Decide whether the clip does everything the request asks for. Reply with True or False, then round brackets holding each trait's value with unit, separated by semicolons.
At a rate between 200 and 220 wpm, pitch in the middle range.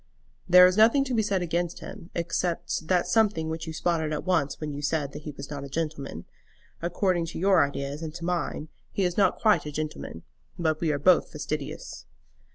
True (205 wpm; 165 Hz)